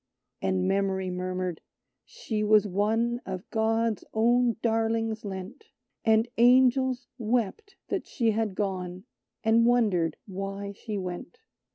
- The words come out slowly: Yes, slow, 120 wpm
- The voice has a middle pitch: No, high, 220 Hz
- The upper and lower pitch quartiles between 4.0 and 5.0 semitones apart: No, average, 3.5 semitones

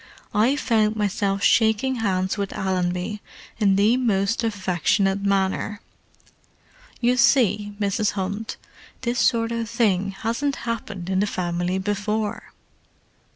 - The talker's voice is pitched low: No, high, 205 Hz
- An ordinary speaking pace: No, slow, 115 wpm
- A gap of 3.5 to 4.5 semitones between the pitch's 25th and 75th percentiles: No, average, 2.9 semitones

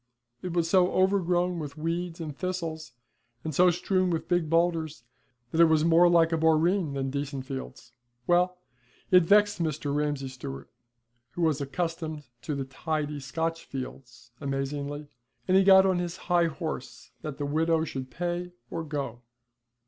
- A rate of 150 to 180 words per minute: Yes, average, 160 wpm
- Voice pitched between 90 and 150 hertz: No, medium, 160 Hz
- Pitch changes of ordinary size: Yes, average, 3.5 semitones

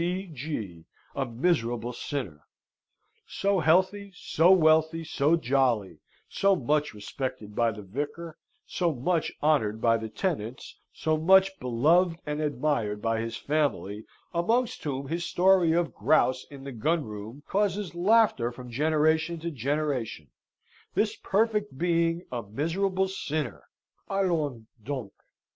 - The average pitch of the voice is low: No, medium, 150 Hz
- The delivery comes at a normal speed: No, slow, 125 wpm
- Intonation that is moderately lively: No, wide, 6.4 semitones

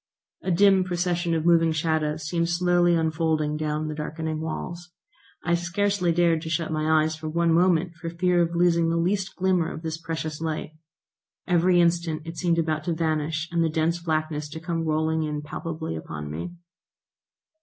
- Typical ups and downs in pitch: No, narrow, 1.7 semitones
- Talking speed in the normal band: Yes, average, 175 wpm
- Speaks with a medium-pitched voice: Yes, medium, 165 Hz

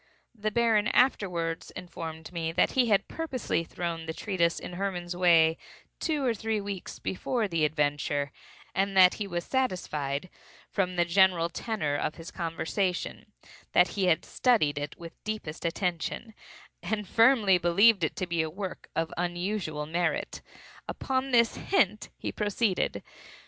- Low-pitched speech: No, medium, 180 Hz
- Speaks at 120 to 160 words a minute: Yes, average, 150 wpm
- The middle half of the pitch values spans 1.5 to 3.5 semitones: No, average, 4.4 semitones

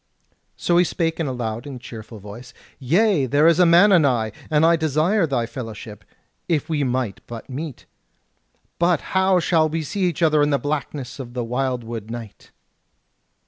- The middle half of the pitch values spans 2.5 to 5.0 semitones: No, wide, 5.4 semitones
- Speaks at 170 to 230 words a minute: Yes, average, 175 wpm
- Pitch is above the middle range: No, medium, 145 Hz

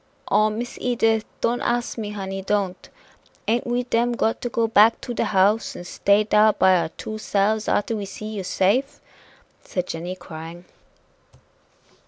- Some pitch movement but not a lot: Yes, average, 3.1 semitones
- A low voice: No, high, 215 Hz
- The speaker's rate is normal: Yes, average, 165 wpm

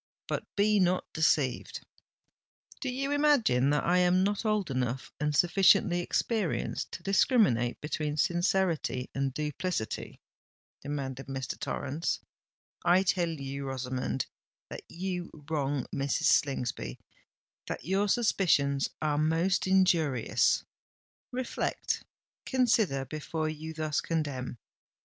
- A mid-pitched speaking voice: Yes, medium, 160 Hz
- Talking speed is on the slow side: Yes, slow, 105 wpm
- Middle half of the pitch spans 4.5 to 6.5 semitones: Yes, wide, 5.6 semitones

